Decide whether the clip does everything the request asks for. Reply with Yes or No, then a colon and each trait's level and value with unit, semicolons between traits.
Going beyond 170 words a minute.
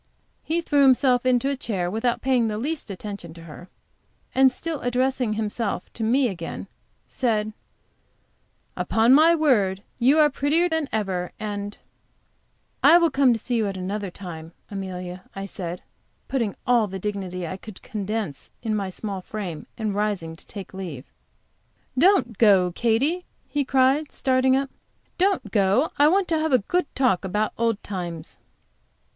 No: average, 160 wpm